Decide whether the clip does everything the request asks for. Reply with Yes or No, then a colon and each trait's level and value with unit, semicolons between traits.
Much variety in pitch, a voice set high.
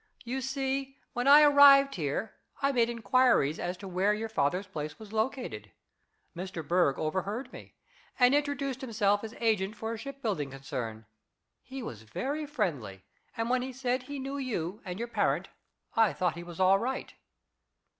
Yes: wide, 6.9 semitones; high, 225 Hz